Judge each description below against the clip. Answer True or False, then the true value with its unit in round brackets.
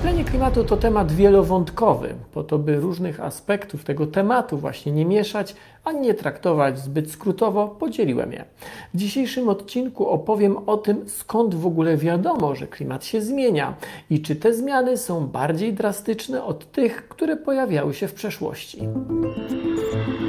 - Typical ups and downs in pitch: False (6.4 semitones)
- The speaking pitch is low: False (200 Hz)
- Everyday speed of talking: True (150 wpm)